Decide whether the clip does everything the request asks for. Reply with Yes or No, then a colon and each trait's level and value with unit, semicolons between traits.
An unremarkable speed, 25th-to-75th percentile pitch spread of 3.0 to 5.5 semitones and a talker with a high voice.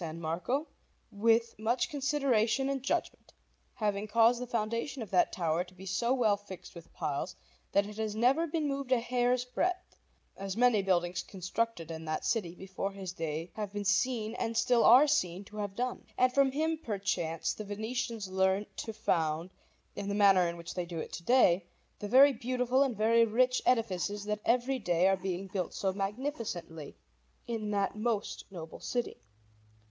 Yes: average, 175 wpm; average, 4.8 semitones; high, 215 Hz